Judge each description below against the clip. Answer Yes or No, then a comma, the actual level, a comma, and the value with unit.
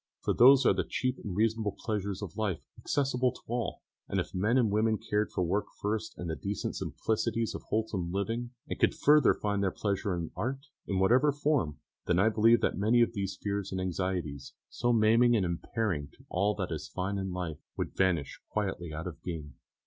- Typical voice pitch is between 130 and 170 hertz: No, low, 100 Hz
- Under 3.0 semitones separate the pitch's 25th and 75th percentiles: No, average, 3.9 semitones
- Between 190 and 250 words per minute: Yes, average, 200 wpm